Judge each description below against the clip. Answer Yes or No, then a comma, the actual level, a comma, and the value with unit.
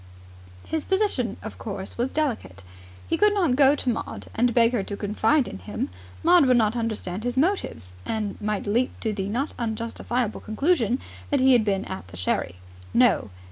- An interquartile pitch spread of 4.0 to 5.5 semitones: Yes, average, 4.5 semitones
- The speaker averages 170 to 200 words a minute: Yes, average, 180 wpm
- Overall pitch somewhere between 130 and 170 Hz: No, high, 230 Hz